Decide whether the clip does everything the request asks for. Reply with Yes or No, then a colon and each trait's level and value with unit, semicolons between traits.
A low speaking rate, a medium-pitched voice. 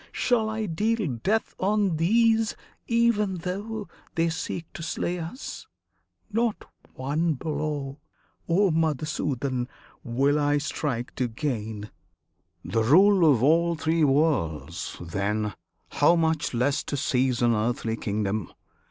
Yes: slow, 120 wpm; medium, 155 Hz